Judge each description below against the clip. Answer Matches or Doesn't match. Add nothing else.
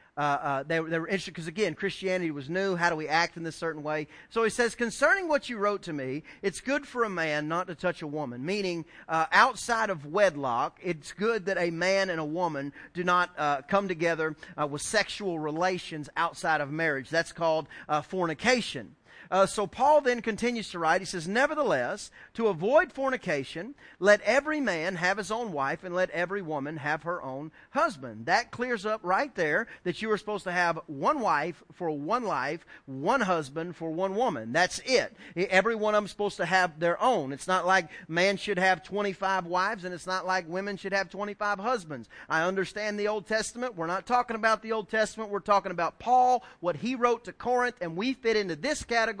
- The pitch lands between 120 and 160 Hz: Doesn't match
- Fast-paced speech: Matches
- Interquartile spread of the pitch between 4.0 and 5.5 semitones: Matches